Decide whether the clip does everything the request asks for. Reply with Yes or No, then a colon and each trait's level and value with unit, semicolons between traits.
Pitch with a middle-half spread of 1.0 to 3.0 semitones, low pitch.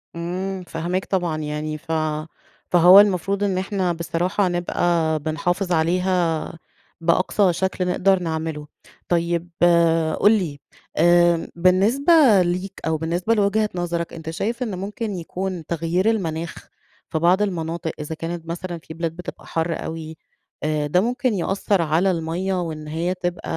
No: narrow, 2.6 semitones; medium, 175 Hz